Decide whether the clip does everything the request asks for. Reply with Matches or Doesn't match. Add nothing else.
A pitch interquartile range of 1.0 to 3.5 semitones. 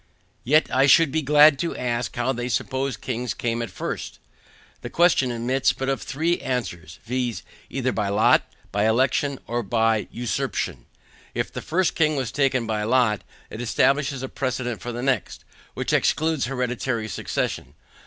Matches